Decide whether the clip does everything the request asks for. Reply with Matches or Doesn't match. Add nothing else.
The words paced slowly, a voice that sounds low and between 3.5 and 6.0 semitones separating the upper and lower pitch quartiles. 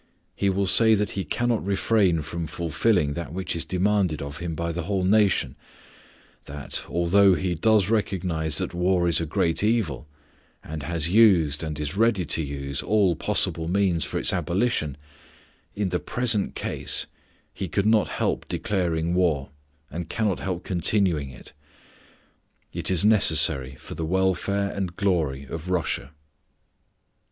Doesn't match